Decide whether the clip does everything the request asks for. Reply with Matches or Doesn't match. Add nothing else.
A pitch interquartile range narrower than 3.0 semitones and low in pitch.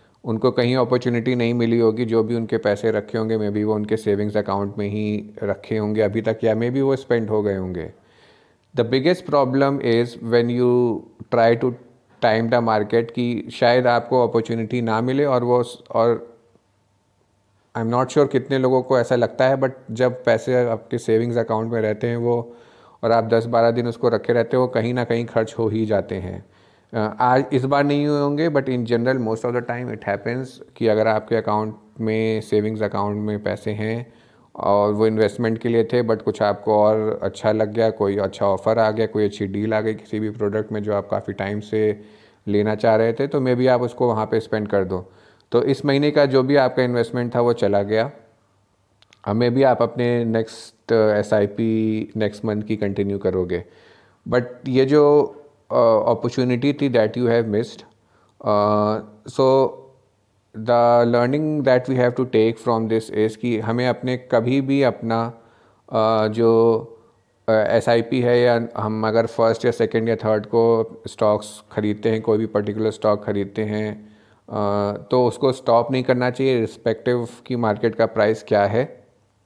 Matches